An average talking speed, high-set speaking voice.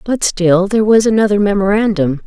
Yes: average, 160 wpm; high, 200 Hz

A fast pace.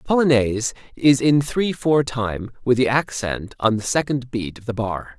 No: average, 195 wpm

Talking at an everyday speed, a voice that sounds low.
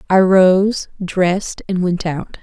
No: average, 150 wpm; medium, 185 Hz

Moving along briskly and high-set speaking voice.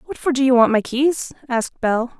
Yes: fast, 245 wpm; very high, 255 Hz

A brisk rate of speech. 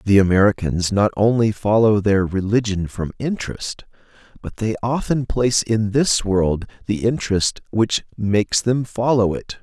No: average, 145 wpm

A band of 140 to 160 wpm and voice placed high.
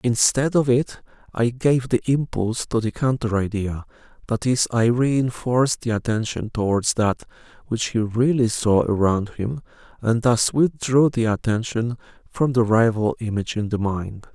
No: average, 155 wpm; low, 115 Hz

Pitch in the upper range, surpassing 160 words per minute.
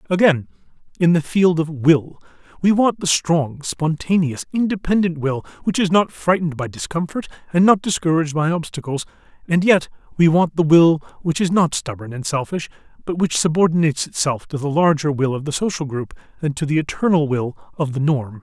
No: medium, 160 Hz; average, 180 wpm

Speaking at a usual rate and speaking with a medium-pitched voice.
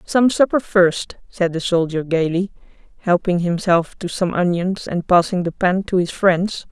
Yes: average, 170 wpm; medium, 180 Hz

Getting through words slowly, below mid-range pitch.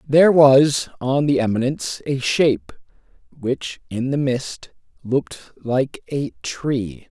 Yes: slow, 125 wpm; low, 130 Hz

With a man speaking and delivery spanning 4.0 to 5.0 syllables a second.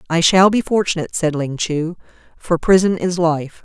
No: female; 4.9 syllables/s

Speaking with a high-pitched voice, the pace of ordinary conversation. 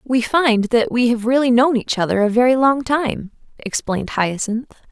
Yes: high, 240 Hz; average, 185 wpm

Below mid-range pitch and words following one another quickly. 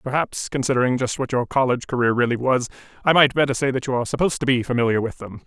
Yes: low, 125 Hz; fast, 240 wpm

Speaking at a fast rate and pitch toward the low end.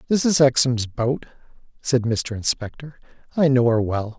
No: average, 160 wpm; low, 125 Hz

